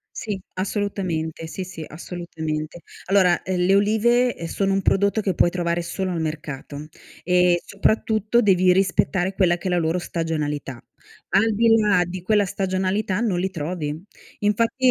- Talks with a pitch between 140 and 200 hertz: Yes, medium, 185 Hz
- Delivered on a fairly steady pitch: No, average, 3.0 semitones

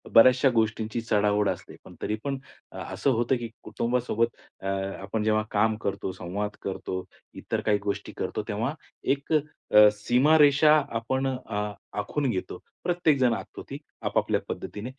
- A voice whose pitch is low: Yes, low, 115 Hz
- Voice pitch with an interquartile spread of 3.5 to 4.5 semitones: Yes, average, 4.1 semitones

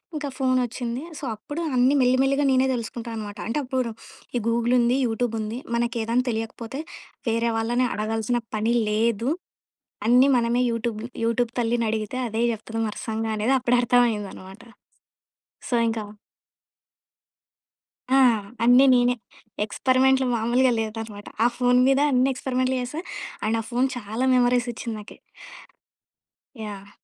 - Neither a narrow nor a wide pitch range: No, narrow, 2.1 semitones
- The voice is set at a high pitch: Yes, high, 235 Hz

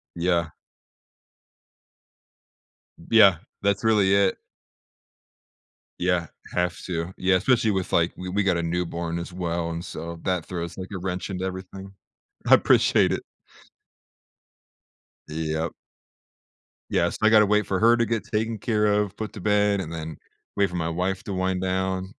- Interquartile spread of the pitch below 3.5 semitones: Yes, average, 2.9 semitones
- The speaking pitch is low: Yes, very low, 95 Hz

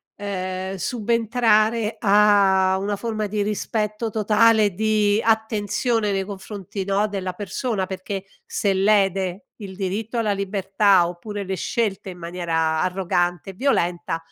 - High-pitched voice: Yes, high, 200 Hz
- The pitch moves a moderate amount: No, narrow, 2.3 semitones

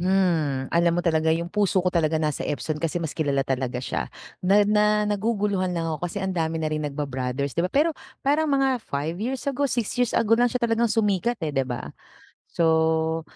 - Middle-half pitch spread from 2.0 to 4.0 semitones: No, average, 5.3 semitones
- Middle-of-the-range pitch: Yes, medium, 170 Hz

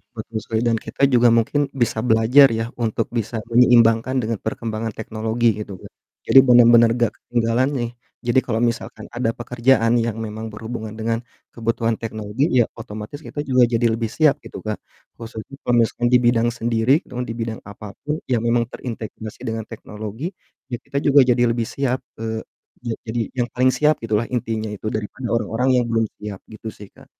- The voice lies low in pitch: Yes, low, 115 Hz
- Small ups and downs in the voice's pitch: Yes, narrow, 1.6 semitones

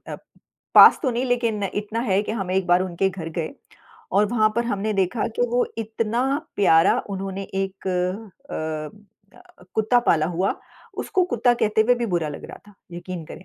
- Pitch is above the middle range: Yes, high, 200 Hz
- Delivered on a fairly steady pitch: No, average, 3.7 semitones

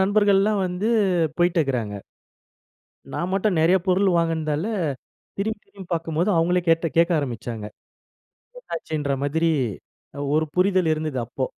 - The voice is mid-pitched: Yes, medium, 165 Hz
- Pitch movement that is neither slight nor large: Yes, average, 3.6 semitones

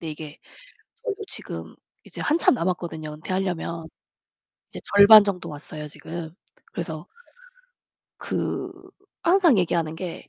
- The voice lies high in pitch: No, medium, 170 Hz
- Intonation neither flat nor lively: Yes, average, 4.1 semitones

